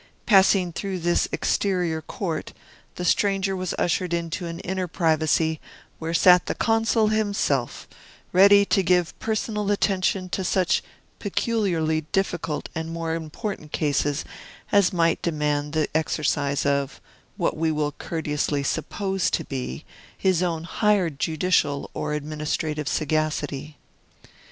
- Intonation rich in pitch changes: No, average, 3.8 semitones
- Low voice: No, medium, 165 Hz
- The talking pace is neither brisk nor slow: No, slow, 125 wpm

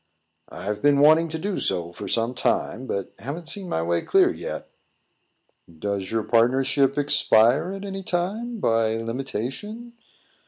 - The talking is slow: No, average, 145 wpm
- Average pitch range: No, wide, 7.9 semitones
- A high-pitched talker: No, low, 135 Hz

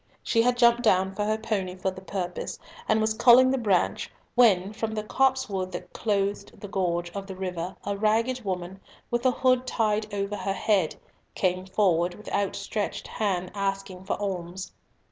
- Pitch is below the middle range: No, high, 200 Hz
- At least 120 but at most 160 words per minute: No, average, 175 wpm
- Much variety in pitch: No, average, 2.8 semitones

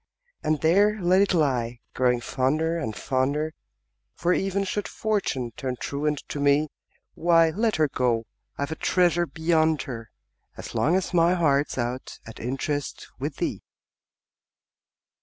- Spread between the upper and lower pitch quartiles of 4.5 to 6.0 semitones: Yes, average, 4.8 semitones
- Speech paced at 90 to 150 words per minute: Yes, average, 140 wpm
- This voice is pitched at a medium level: Yes, medium, 155 Hz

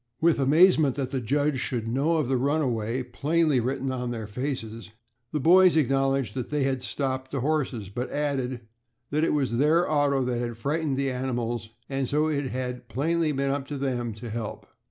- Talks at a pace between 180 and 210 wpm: Yes, average, 190 wpm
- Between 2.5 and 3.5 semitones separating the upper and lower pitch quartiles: Yes, average, 3.1 semitones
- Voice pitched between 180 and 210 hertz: No, low, 135 Hz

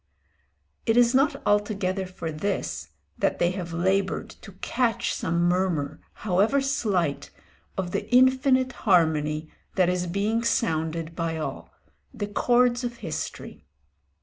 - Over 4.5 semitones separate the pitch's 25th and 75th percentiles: Yes, wide, 5.6 semitones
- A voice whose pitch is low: No, high, 190 Hz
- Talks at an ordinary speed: No, slow, 125 wpm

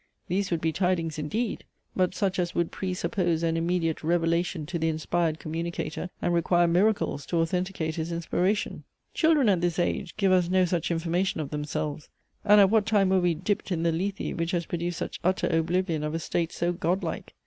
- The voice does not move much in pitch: Yes, narrow, 2.2 semitones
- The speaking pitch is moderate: Yes, medium, 175 Hz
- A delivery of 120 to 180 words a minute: No, average, 195 wpm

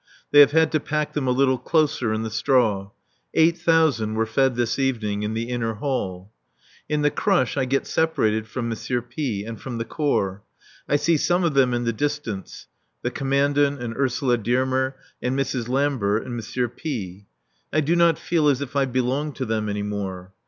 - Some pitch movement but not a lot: Yes, average, 4.5 semitones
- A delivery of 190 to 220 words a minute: Yes, average, 195 wpm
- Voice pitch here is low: Yes, low, 130 Hz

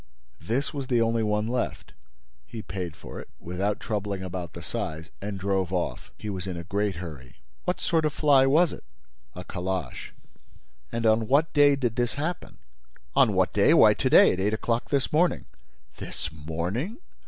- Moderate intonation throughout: No, wide, 6.5 semitones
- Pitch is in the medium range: No, low, 105 Hz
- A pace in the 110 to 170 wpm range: No, average, 180 wpm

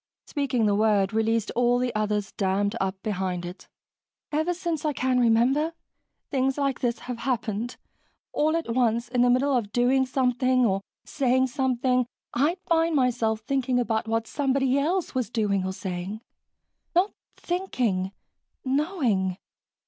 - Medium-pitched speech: No, high, 245 Hz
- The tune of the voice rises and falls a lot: No, average, 3.9 semitones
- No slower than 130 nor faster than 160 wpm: Yes, average, 145 wpm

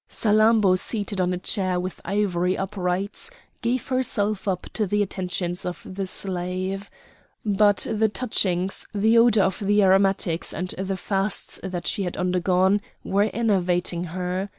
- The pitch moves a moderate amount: No, narrow, 2.3 semitones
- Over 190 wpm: No, average, 145 wpm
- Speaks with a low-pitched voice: No, high, 195 Hz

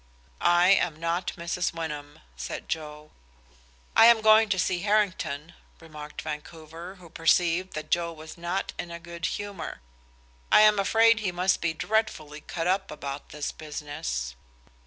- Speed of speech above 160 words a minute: No, average, 150 wpm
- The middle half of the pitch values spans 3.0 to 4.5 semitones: Yes, average, 3.6 semitones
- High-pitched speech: No, medium, 170 Hz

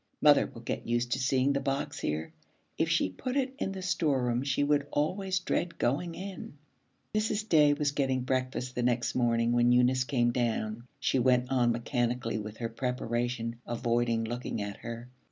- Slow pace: No, average, 175 wpm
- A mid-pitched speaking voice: No, low, 125 Hz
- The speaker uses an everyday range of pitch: Yes, average, 3.3 semitones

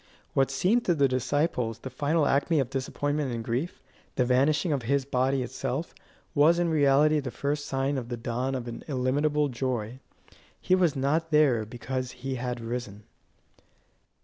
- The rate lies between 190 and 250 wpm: No, average, 165 wpm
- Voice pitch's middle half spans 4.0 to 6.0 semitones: No, average, 2.9 semitones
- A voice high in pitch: No, low, 135 Hz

